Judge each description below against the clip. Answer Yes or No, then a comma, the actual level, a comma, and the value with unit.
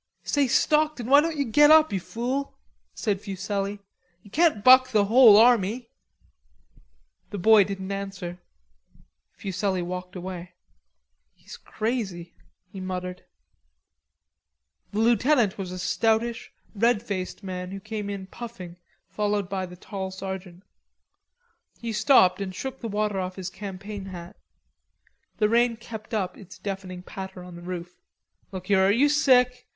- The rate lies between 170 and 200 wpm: No, average, 140 wpm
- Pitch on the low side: No, high, 200 Hz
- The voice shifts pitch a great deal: No, average, 3.9 semitones